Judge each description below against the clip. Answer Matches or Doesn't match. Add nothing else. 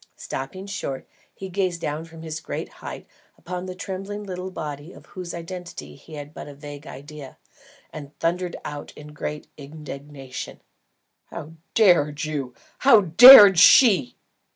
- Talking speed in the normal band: Matches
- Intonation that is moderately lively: Matches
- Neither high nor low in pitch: Matches